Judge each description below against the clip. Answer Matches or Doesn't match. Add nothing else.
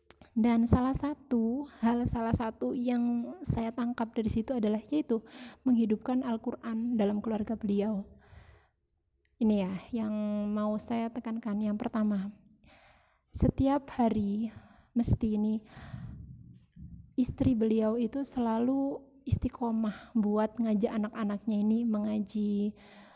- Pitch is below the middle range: Doesn't match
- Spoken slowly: Matches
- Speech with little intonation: Matches